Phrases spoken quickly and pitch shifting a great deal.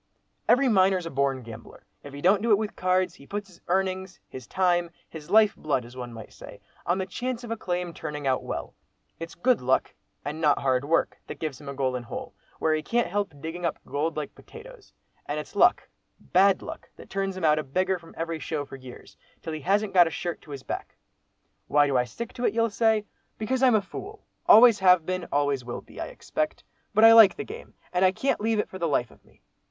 Yes: fast, 235 wpm; wide, 6.2 semitones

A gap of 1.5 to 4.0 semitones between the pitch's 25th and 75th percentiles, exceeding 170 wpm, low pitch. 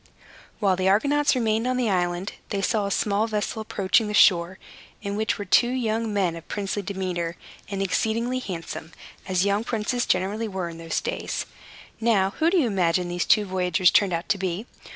No: average, 3.3 semitones; average, 190 wpm; high, 200 Hz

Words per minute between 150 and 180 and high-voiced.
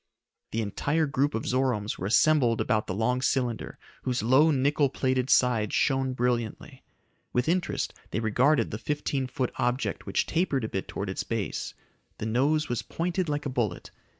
No: average, 170 wpm; low, 130 Hz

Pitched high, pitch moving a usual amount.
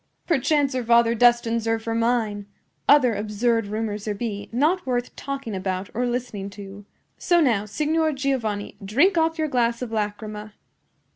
Yes: high, 230 Hz; average, 4.1 semitones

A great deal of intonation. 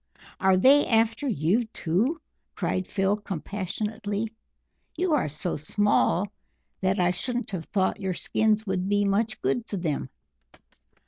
No: average, 3.2 semitones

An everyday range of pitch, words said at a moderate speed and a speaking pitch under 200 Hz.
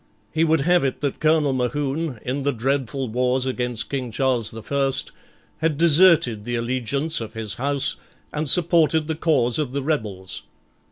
Yes: average, 3.9 semitones; average, 165 wpm; low, 135 Hz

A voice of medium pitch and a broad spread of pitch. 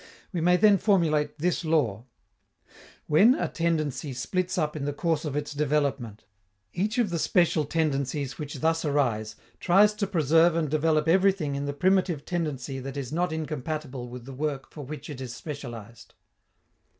No: medium, 150 Hz; average, 3.6 semitones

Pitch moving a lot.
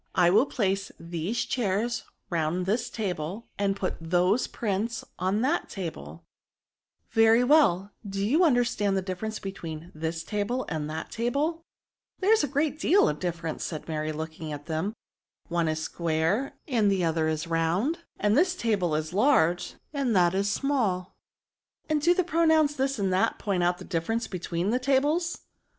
Yes: wide, 6.7 semitones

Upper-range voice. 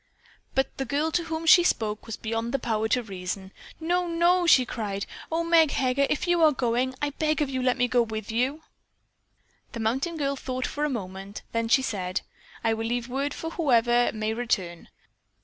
Yes: very high, 250 Hz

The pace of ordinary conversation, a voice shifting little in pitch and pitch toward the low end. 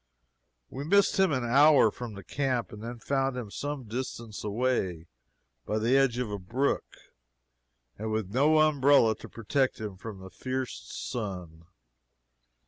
No: average, 150 wpm; average, 4.4 semitones; low, 120 Hz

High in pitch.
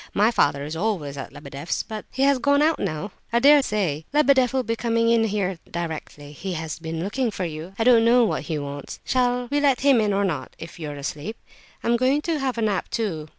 Yes: high, 210 Hz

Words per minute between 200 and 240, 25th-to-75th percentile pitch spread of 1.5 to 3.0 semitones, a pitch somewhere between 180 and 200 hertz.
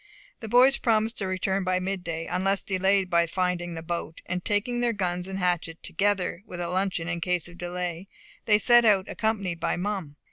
No: average, 190 wpm; narrow, 2.6 semitones; medium, 185 Hz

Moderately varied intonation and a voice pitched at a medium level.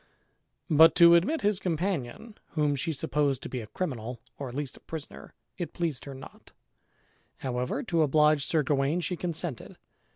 Yes: average, 4.1 semitones; medium, 150 Hz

